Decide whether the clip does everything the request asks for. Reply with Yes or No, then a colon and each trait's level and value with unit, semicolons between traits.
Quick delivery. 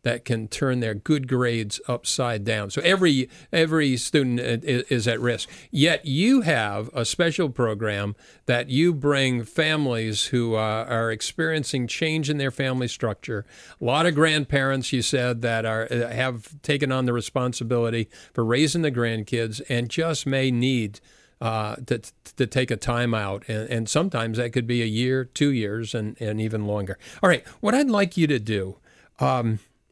No: average, 175 wpm